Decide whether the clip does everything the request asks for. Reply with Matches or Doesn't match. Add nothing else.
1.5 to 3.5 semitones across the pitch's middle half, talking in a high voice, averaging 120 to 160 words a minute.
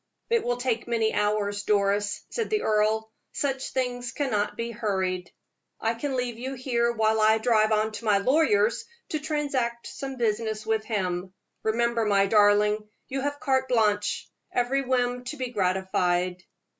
Matches